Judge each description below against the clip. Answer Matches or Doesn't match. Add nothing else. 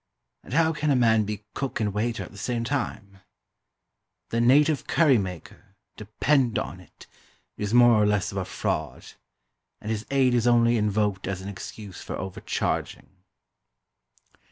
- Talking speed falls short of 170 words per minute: Matches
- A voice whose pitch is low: Matches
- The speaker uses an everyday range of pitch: Matches